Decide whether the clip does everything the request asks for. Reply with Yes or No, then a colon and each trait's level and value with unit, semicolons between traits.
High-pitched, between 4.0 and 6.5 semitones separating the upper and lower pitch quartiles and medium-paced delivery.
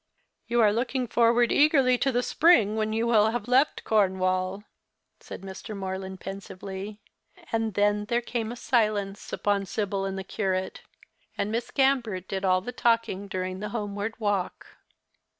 No: high, 210 Hz; average, 3.3 semitones; average, 155 wpm